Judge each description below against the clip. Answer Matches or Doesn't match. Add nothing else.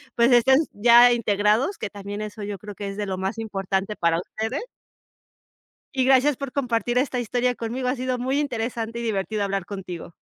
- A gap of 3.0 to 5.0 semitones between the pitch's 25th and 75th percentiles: Matches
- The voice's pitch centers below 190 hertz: Doesn't match